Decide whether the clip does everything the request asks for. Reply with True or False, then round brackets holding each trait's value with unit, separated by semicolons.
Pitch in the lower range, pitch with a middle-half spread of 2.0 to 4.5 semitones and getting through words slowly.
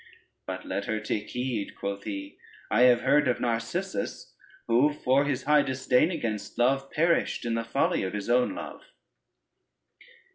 False (125 Hz; 3.9 semitones; 155 wpm)